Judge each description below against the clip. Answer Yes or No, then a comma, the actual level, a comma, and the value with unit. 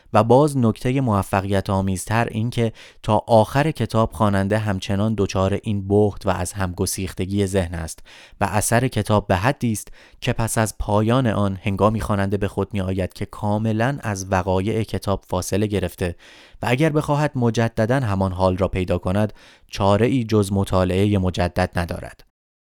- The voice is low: Yes, low, 100 Hz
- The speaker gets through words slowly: No, fast, 155 wpm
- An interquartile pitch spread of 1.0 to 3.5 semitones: Yes, average, 2.8 semitones